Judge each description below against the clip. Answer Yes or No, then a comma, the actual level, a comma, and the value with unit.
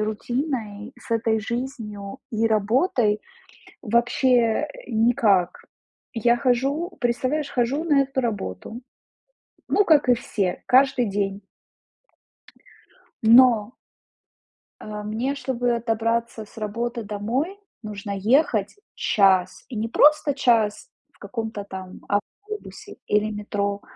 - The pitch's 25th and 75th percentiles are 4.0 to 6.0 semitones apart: No, average, 3.6 semitones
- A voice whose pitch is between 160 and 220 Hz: No, high, 230 Hz